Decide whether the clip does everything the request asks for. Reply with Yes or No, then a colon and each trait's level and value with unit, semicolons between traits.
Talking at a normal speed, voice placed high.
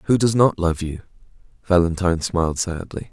No: average, 155 wpm; very low, 90 Hz